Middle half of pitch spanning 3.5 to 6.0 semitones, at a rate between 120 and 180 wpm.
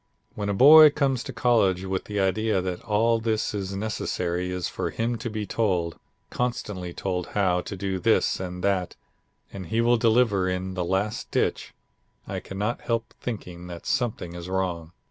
Yes: average, 3.8 semitones; average, 175 wpm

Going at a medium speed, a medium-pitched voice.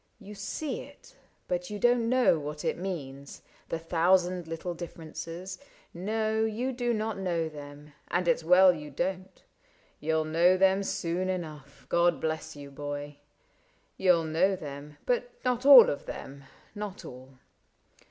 Yes: average, 160 wpm; medium, 175 Hz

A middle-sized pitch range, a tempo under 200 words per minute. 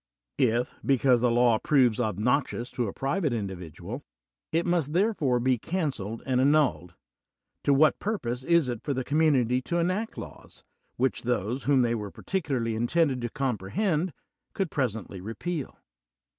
Yes: average, 4.8 semitones; average, 150 wpm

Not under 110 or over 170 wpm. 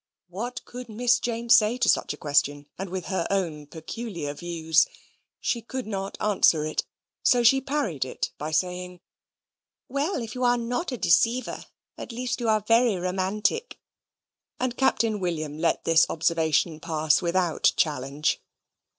Yes: average, 150 wpm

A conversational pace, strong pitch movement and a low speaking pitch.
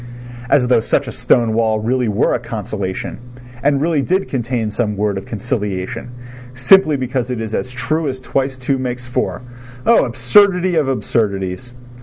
No: average, 165 wpm; average, 3.4 semitones; low, 125 Hz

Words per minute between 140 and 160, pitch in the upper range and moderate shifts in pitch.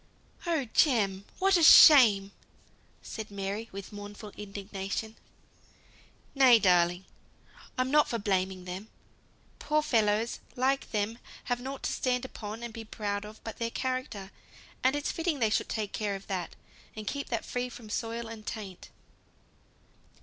Yes: average, 150 wpm; high, 220 Hz; average, 4.0 semitones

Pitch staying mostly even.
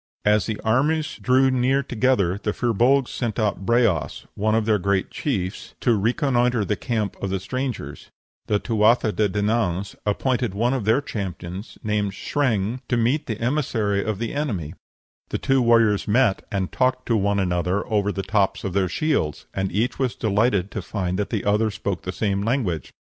No: average, 3.9 semitones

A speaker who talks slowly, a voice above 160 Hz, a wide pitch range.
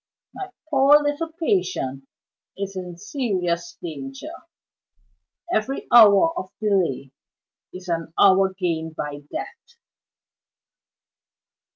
Yes: slow, 90 wpm; high, 190 Hz; wide, 8.5 semitones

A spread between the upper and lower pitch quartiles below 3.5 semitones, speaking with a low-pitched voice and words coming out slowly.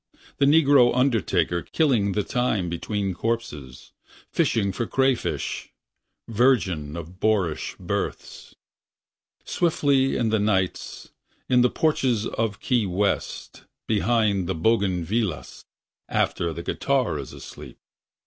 No: average, 5.2 semitones; low, 110 Hz; slow, 110 wpm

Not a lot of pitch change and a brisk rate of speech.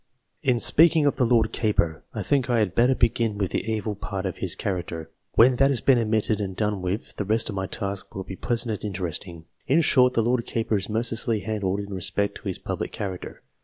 No: average, 3.5 semitones; fast, 225 wpm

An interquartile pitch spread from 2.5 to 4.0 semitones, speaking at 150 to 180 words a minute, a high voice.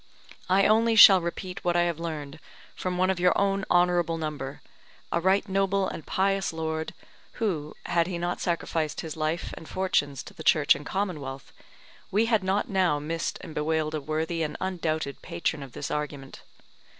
No: average, 3.5 semitones; average, 175 wpm; medium, 170 Hz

